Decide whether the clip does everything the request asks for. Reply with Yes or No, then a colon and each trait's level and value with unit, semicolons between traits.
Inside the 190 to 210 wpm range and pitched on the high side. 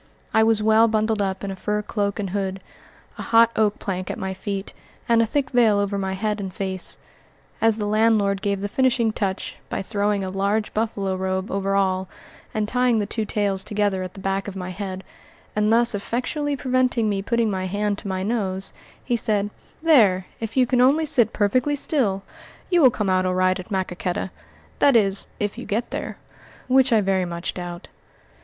Yes: average, 200 wpm; high, 205 Hz